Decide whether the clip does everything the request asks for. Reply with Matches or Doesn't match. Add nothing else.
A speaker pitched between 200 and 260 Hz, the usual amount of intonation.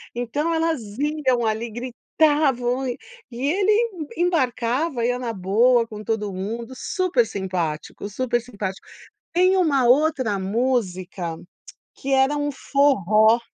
Matches